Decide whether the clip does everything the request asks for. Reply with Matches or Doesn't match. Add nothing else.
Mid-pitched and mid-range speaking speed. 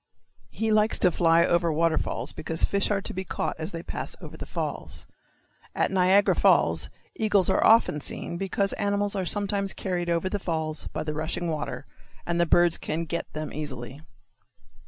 Matches